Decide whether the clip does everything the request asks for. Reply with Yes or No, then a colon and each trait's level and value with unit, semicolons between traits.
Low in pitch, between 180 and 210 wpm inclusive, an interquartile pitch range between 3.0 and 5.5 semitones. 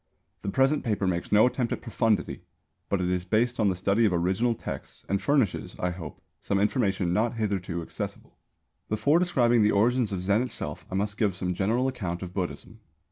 Yes: low, 105 Hz; average, 190 wpm; average, 4.3 semitones